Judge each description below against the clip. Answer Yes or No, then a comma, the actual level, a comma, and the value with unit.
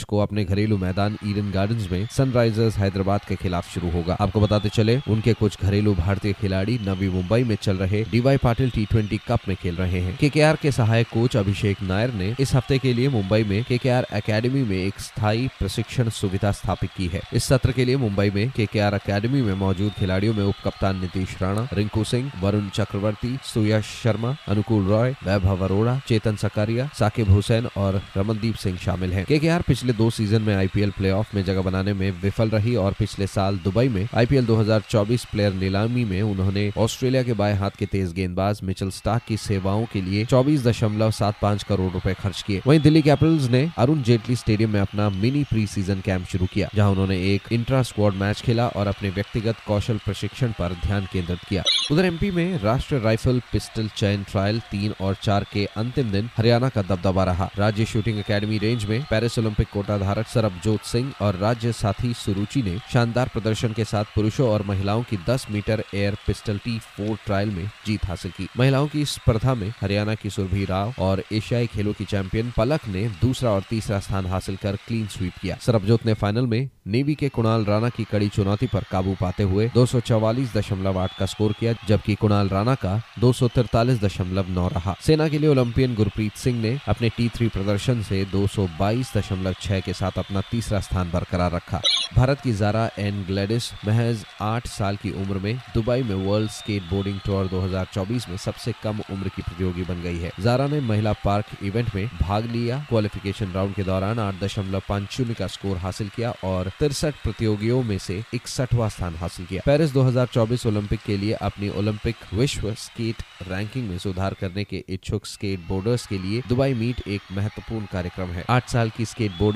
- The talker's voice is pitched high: No, low, 105 Hz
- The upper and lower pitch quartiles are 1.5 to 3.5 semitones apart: Yes, average, 3.1 semitones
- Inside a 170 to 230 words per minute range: Yes, average, 185 wpm